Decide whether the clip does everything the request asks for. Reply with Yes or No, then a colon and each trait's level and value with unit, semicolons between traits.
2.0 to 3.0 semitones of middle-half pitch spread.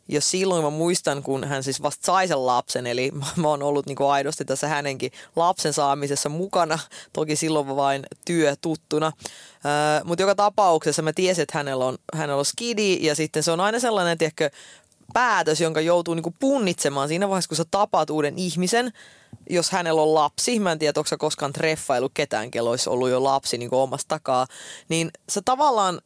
No: average, 3.7 semitones